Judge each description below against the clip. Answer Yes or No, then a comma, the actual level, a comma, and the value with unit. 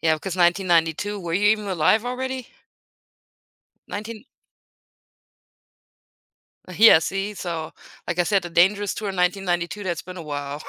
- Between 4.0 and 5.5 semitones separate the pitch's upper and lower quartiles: No, average, 3.4 semitones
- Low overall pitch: No, medium, 185 Hz